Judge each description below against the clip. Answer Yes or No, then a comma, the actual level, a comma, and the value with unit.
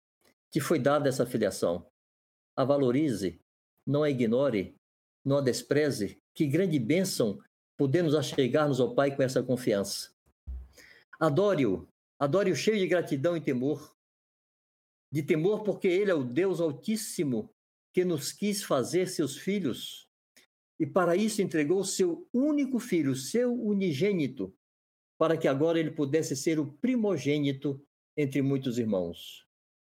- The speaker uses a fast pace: No, average, 135 wpm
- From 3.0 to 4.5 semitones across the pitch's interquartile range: No, average, 5.3 semitones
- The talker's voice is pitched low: No, medium, 150 Hz